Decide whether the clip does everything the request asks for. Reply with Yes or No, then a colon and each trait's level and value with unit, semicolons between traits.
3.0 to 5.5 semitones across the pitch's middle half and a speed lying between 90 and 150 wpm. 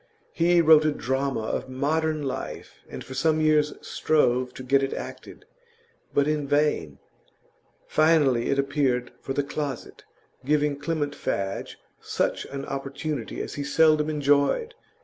No: narrow, 2.4 semitones; average, 140 wpm